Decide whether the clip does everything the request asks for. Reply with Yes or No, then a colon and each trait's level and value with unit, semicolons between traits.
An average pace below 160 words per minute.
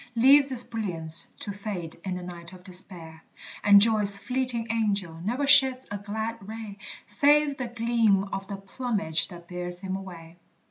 No: average, 165 wpm